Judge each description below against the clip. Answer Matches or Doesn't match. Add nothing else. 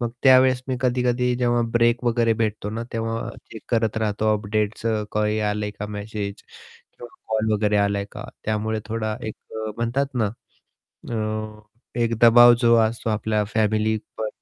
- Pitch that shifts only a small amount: Matches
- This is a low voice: Matches